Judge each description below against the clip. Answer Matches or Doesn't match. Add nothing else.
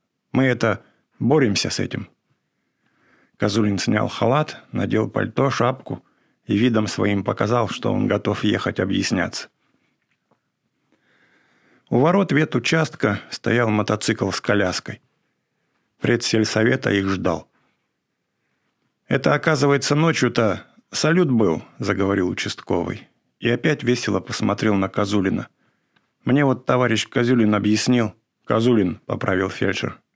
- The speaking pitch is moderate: Doesn't match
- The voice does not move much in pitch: Doesn't match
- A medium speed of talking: Doesn't match